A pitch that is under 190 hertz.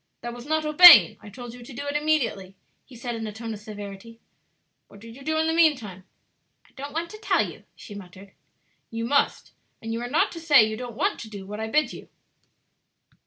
No: high, 235 Hz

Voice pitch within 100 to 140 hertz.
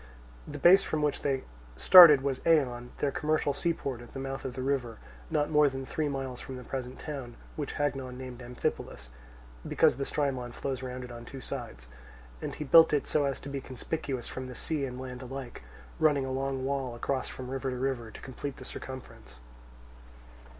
Yes: low, 135 Hz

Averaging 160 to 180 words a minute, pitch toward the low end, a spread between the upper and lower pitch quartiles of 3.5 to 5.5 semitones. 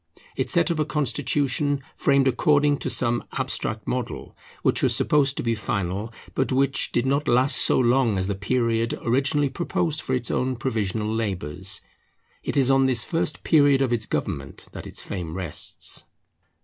Yes: average, 170 wpm; low, 130 Hz; average, 4.2 semitones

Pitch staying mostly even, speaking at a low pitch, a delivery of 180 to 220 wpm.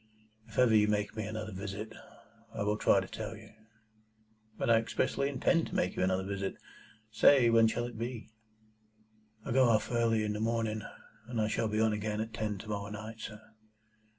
Yes: narrow, 1.5 semitones; low, 110 Hz; average, 195 wpm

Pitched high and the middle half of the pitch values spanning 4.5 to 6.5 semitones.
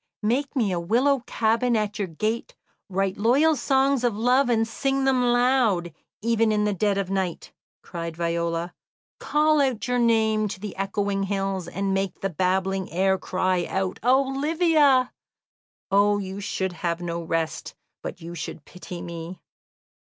Yes: high, 205 Hz; average, 5.1 semitones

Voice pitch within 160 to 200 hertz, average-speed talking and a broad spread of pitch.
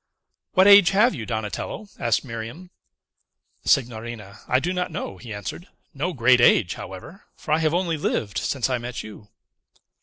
No: low, 125 Hz; average, 160 wpm; wide, 8.0 semitones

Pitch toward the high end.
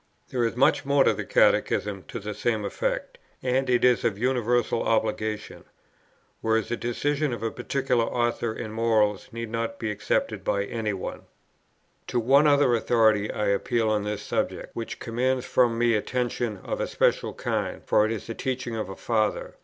No: low, 115 Hz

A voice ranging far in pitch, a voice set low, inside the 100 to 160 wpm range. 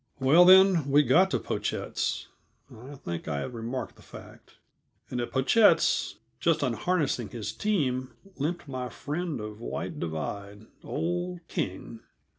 Yes: wide, 7.3 semitones; low, 130 Hz; slow, 135 wpm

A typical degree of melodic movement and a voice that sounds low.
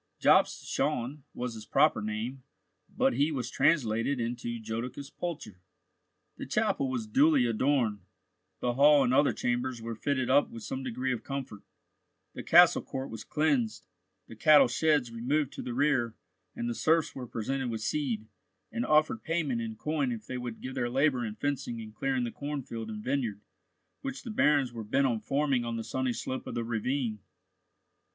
Yes: average, 3.5 semitones; low, 125 Hz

